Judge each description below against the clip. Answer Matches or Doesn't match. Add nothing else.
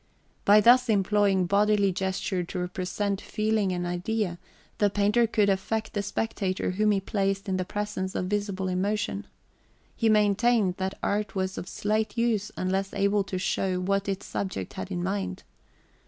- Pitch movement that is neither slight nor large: Doesn't match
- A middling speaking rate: Matches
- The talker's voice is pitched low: Doesn't match